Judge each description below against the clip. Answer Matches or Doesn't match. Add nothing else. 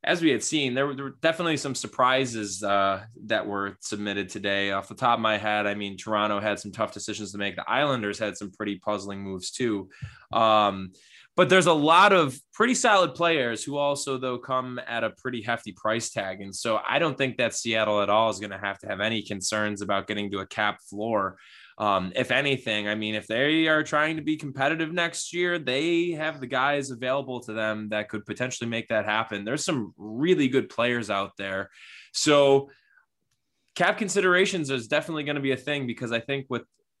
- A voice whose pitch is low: Matches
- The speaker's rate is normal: Doesn't match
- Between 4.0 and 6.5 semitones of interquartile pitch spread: Matches